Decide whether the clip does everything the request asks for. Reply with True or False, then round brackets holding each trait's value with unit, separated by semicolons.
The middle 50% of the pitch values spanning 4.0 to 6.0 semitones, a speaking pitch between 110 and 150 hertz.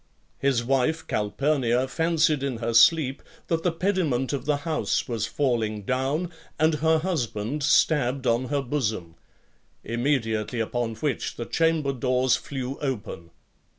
True (4.4 semitones; 135 Hz)